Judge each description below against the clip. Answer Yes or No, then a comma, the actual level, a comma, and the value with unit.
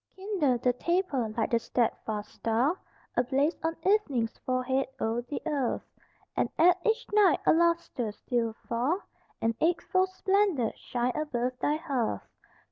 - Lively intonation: Yes, wide, 6.4 semitones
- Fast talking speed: No, slow, 135 wpm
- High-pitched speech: Yes, very high, 270 Hz